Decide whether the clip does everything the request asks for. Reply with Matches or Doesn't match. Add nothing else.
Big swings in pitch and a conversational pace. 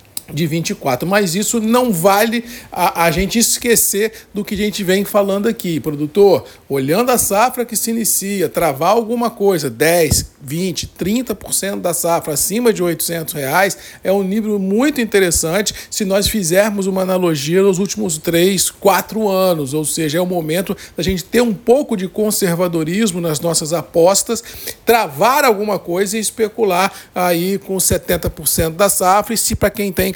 Doesn't match